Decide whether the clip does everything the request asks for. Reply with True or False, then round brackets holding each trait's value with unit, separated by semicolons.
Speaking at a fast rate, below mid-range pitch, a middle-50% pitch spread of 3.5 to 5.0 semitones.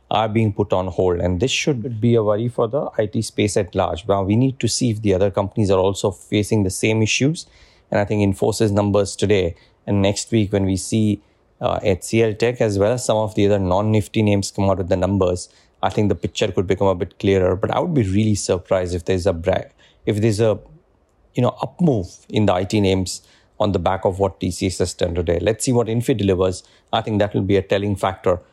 False (240 wpm; 105 Hz; 2.8 semitones)